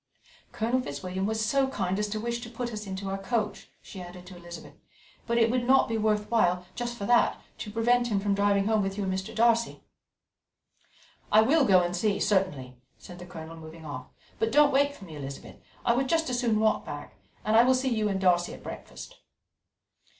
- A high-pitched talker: Yes, high, 210 Hz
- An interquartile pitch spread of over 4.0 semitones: Yes, average, 4.5 semitones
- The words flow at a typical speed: No, fast, 215 wpm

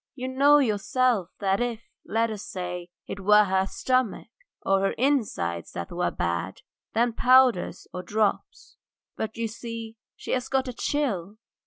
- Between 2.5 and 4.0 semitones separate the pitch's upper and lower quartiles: No, average, 4.8 semitones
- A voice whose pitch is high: Yes, high, 220 Hz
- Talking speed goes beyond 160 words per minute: No, average, 155 wpm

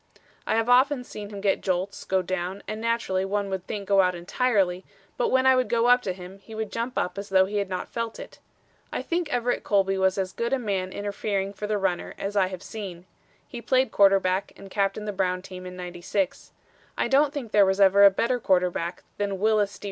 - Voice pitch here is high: Yes, high, 200 Hz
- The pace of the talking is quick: Yes, fast, 225 wpm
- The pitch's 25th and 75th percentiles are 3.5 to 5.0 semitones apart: No, average, 3.1 semitones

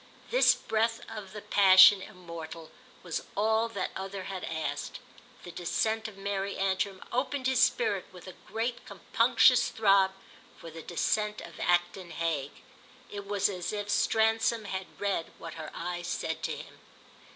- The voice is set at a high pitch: Yes, high, 195 Hz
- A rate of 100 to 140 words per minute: No, average, 150 wpm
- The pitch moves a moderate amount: Yes, average, 3.7 semitones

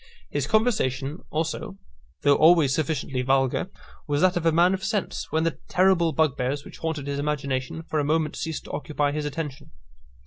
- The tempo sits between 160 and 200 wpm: Yes, average, 175 wpm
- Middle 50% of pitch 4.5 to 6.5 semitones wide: No, average, 2.7 semitones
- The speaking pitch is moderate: Yes, medium, 155 Hz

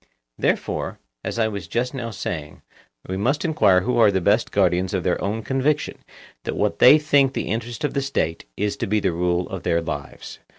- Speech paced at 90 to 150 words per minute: No, fast, 205 wpm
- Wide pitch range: Yes, wide, 5.9 semitones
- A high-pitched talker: No, low, 105 Hz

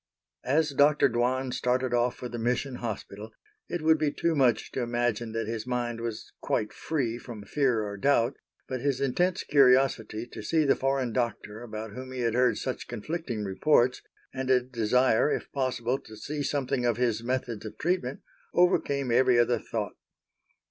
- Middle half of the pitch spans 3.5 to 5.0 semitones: No, average, 2.7 semitones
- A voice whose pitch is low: Yes, low, 125 Hz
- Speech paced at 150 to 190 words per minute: Yes, average, 175 wpm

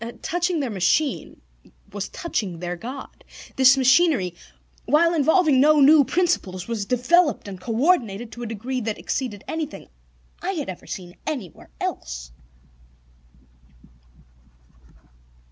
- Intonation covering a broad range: Yes, wide, 7.5 semitones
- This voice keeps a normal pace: No, slow, 115 wpm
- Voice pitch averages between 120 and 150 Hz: No, very high, 255 Hz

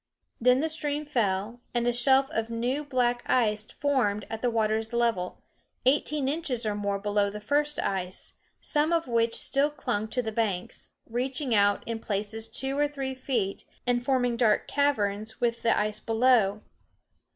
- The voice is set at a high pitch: Yes, high, 235 Hz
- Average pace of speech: Yes, average, 165 wpm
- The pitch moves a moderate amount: Yes, average, 4.0 semitones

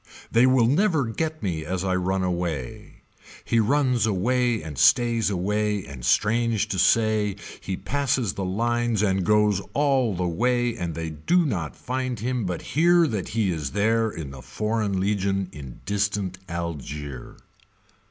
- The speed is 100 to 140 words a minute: No, average, 155 wpm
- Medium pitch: No, low, 105 Hz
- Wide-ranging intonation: No, average, 4.7 semitones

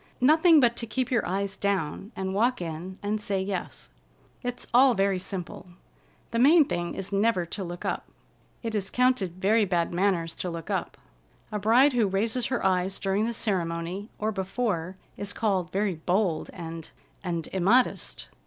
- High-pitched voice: Yes, high, 195 Hz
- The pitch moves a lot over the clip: No, average, 4.2 semitones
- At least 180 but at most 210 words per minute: No, average, 165 wpm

